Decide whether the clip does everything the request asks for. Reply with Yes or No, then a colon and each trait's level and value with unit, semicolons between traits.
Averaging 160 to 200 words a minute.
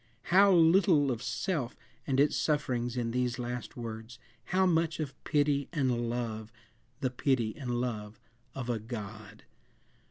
No: average, 140 wpm